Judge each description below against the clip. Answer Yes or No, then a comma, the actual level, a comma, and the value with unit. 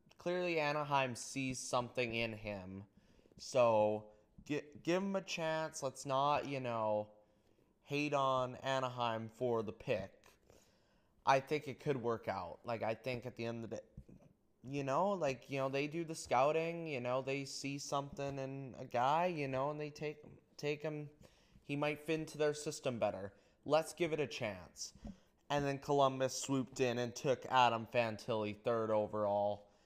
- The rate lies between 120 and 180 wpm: Yes, average, 170 wpm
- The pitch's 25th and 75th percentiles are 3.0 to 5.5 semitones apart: Yes, average, 4.2 semitones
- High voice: No, low, 135 Hz